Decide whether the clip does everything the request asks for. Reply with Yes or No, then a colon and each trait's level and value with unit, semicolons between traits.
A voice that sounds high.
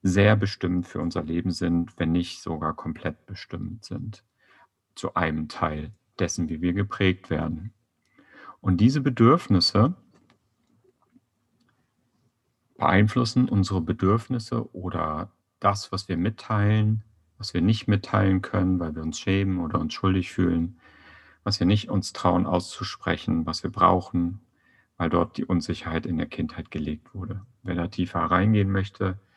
No: very low, 95 Hz